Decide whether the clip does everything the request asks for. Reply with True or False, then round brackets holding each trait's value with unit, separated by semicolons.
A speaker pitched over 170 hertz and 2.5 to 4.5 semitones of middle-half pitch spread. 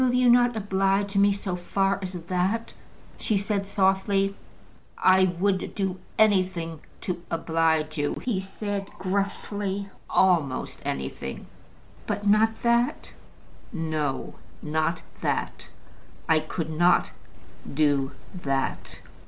True (190 Hz; 3.6 semitones)